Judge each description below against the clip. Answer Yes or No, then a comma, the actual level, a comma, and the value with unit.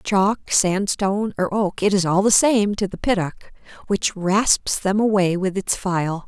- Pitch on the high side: Yes, high, 195 Hz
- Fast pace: No, average, 180 wpm